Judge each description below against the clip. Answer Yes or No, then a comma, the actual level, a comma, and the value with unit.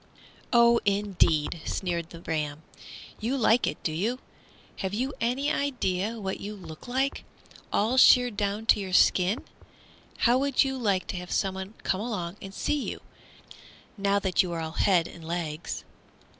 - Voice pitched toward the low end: No, high, 200 Hz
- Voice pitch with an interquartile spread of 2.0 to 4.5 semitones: No, average, 5.0 semitones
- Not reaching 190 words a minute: Yes, average, 160 wpm